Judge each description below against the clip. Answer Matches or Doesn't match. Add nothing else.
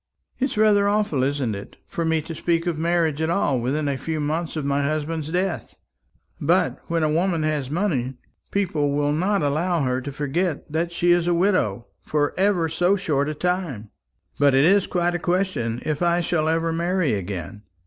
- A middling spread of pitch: Matches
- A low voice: Doesn't match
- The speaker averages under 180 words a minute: Doesn't match